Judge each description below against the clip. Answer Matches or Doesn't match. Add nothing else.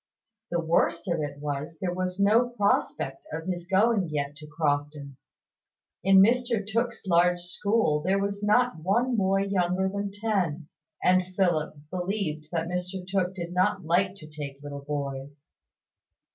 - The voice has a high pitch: Doesn't match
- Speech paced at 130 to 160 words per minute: Matches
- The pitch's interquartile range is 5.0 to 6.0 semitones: Doesn't match